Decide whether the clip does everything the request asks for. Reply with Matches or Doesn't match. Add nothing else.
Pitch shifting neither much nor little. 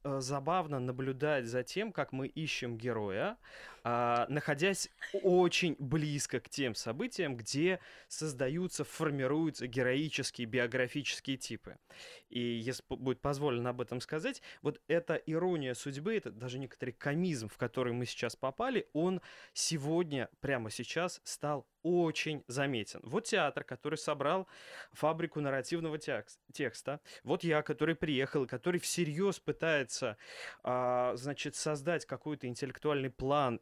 Matches